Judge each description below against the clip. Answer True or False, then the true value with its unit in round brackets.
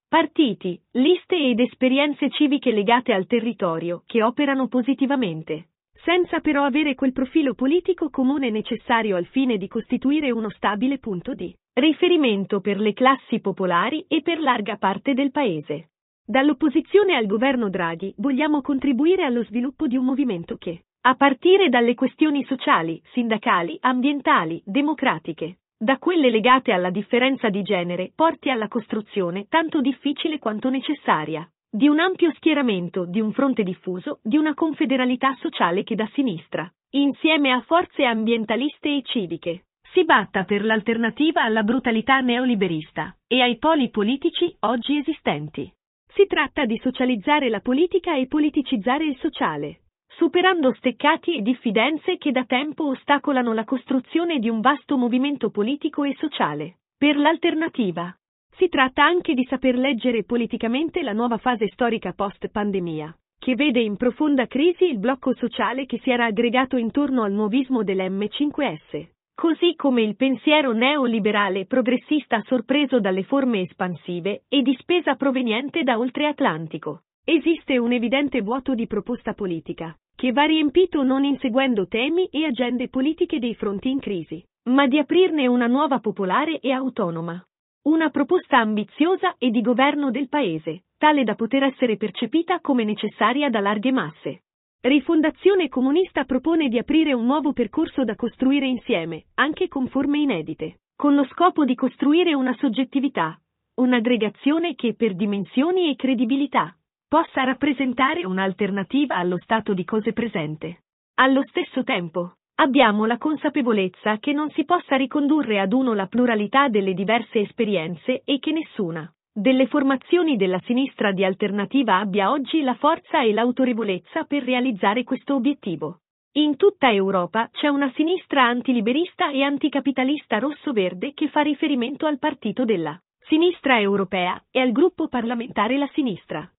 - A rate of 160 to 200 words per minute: False (140 wpm)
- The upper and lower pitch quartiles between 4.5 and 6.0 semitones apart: True (5.0 semitones)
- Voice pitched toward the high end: True (255 Hz)